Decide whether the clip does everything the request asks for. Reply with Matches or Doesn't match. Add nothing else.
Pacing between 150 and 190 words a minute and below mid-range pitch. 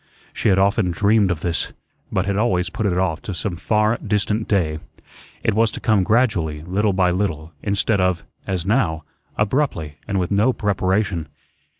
Matches